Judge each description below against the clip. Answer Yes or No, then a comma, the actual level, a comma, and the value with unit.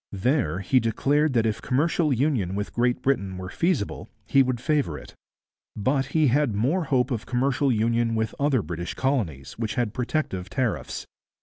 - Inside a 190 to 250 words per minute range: No, average, 170 wpm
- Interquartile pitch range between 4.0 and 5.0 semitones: Yes, average, 4.6 semitones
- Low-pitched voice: Yes, low, 125 Hz